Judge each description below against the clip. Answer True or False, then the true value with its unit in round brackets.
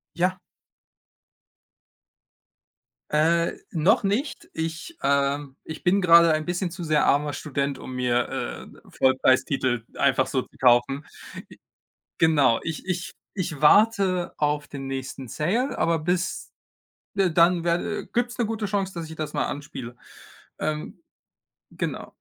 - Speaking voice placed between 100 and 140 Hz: False (160 Hz)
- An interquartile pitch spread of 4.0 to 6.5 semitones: True (4.5 semitones)